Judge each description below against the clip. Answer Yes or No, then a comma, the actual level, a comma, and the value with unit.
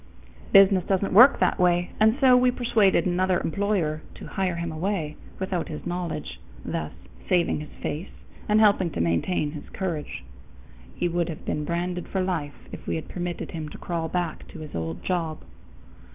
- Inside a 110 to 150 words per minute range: No, average, 175 wpm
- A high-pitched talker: No, medium, 175 Hz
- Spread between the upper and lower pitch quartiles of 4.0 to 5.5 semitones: No, average, 3.3 semitones